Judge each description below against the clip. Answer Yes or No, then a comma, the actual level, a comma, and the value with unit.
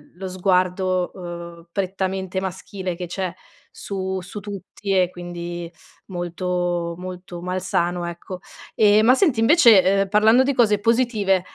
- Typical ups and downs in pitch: No, narrow, 2.3 semitones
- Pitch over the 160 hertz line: Yes, medium, 185 Hz